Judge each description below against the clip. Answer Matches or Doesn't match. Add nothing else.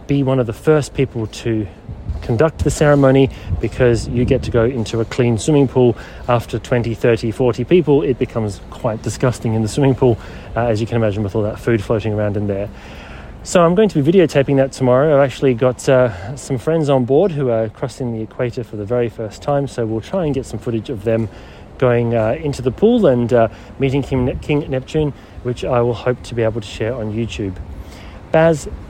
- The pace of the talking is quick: Matches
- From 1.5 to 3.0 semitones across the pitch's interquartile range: Doesn't match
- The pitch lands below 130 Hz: Matches